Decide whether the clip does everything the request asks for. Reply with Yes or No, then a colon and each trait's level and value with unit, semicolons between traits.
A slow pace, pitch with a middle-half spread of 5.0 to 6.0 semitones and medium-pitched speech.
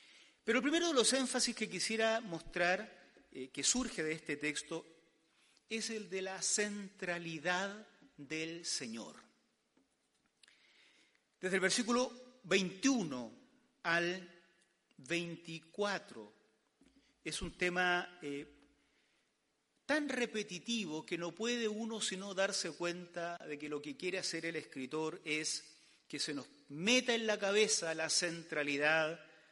Yes: slow, 120 wpm; wide, 5.5 semitones; medium, 180 Hz